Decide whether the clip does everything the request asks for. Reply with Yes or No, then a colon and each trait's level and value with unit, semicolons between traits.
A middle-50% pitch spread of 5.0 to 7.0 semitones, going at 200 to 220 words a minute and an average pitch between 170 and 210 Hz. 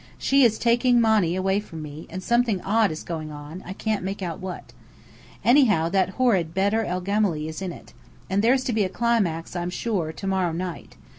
No: average, 4.6 semitones; fast, 205 wpm; high, 190 Hz